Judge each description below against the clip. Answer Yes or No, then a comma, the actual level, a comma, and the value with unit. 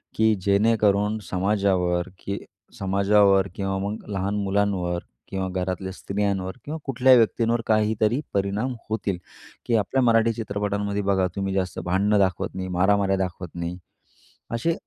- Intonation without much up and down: Yes, narrow, 2.2 semitones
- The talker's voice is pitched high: No, low, 100 Hz